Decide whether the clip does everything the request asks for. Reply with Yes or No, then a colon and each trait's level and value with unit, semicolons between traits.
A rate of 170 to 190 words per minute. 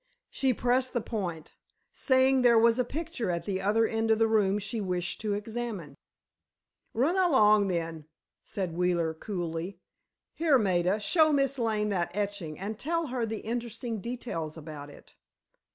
No: average, 155 wpm